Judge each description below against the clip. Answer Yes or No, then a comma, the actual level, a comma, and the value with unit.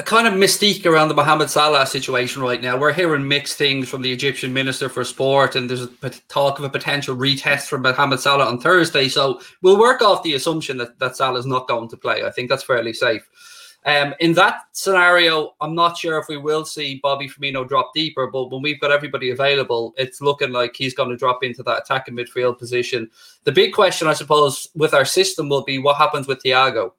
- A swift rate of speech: Yes, fast, 220 wpm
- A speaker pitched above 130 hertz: Yes, medium, 140 Hz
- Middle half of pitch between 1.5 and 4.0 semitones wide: Yes, average, 2.9 semitones